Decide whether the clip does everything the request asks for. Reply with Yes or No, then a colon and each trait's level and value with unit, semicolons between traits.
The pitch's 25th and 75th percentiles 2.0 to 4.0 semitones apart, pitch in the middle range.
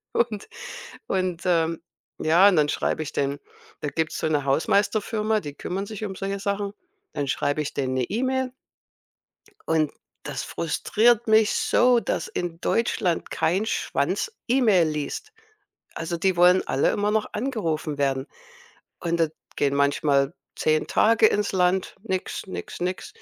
No: wide, 5.5 semitones; medium, 180 Hz